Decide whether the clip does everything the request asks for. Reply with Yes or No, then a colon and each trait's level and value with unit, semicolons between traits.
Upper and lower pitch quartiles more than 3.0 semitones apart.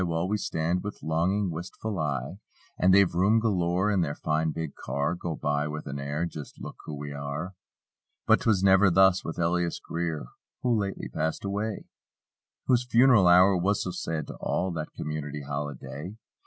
Yes: average, 4.1 semitones